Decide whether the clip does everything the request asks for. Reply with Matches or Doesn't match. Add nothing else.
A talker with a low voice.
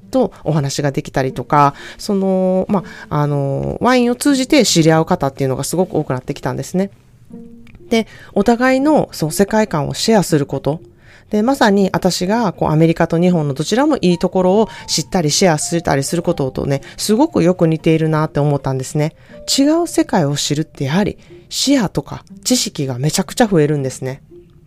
Doesn't match